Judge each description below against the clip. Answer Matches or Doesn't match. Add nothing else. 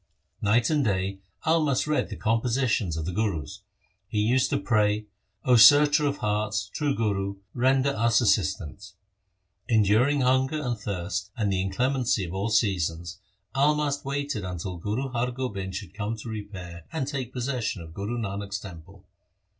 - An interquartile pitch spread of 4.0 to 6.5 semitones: Matches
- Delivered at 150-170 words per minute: Matches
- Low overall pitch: Matches